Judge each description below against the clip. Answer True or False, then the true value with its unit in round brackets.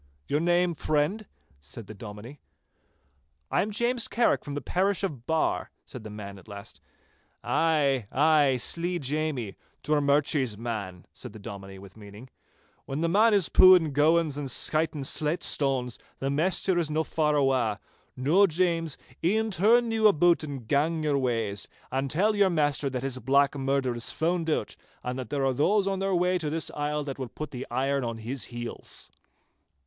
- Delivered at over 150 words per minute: True (175 wpm)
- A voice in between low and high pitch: True (145 Hz)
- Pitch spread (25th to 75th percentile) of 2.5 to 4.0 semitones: False (5.1 semitones)